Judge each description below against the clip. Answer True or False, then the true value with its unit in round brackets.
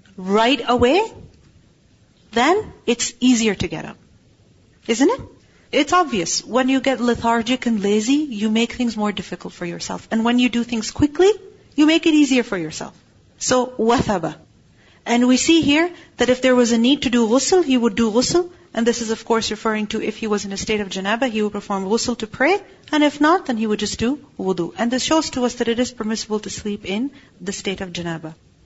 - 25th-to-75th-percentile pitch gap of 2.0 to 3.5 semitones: False (4.0 semitones)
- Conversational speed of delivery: False (215 wpm)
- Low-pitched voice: False (235 Hz)